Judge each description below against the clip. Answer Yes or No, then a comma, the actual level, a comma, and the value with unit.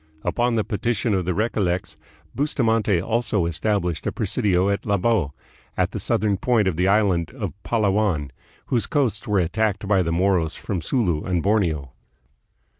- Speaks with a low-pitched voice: Yes, low, 100 Hz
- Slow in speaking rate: No, average, 155 wpm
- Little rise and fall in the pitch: No, average, 3.8 semitones